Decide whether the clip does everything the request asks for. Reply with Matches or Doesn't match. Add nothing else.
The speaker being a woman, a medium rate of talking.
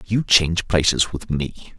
Doesn't match